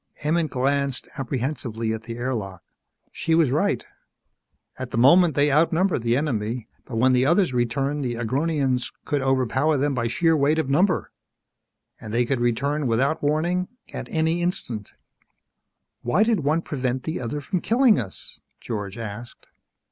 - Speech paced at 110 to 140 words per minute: No, average, 155 wpm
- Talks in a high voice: No, low, 135 Hz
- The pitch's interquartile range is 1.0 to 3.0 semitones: No, average, 4.8 semitones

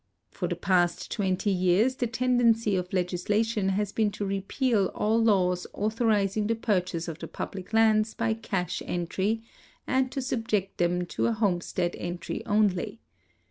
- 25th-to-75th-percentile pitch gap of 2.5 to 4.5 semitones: Yes, average, 3.6 semitones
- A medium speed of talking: Yes, average, 145 wpm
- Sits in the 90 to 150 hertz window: No, high, 205 Hz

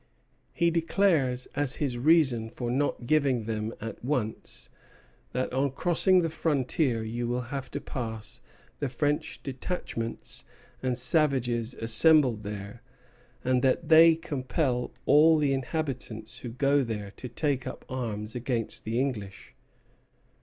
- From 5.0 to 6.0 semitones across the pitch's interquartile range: No, average, 4.1 semitones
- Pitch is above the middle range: No, low, 130 Hz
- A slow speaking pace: Yes, slow, 130 wpm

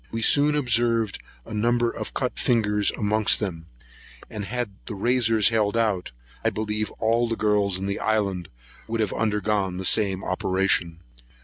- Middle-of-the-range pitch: No, low, 105 Hz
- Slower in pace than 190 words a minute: Yes, average, 155 wpm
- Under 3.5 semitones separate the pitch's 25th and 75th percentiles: Yes, average, 2.7 semitones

